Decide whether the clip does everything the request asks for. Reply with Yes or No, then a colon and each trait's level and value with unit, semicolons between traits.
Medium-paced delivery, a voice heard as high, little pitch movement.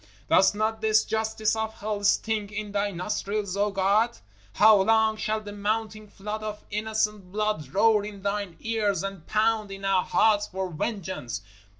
Yes: average, 170 wpm; high, 210 Hz; narrow, 1.6 semitones